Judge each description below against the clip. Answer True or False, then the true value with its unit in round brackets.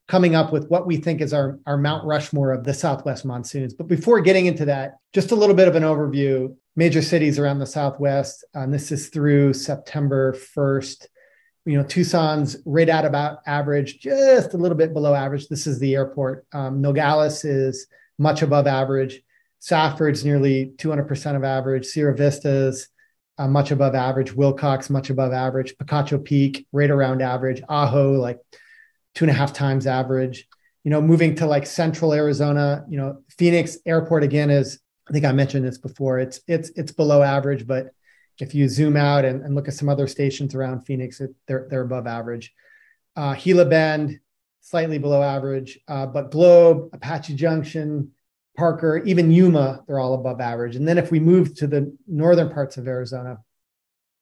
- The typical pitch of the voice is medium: True (145 Hz)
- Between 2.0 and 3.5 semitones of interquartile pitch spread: True (2.7 semitones)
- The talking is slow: False (180 wpm)